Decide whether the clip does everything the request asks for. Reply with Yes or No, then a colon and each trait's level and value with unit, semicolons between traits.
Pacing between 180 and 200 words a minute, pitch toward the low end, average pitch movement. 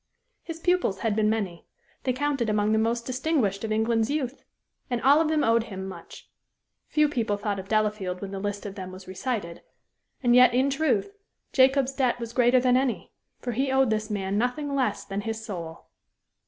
No: average, 195 wpm; high, 230 Hz; average, 4.4 semitones